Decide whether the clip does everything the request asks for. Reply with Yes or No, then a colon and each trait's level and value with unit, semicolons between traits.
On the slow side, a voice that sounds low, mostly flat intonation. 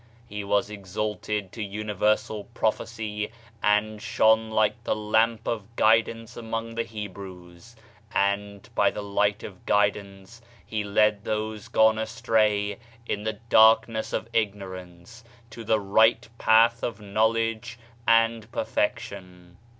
Yes: slow, 125 wpm; low, 105 Hz; narrow, 1.8 semitones